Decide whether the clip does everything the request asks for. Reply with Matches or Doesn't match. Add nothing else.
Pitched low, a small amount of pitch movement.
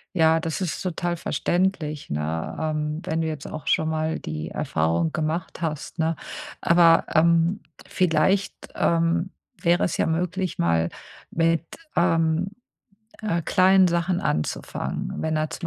Doesn't match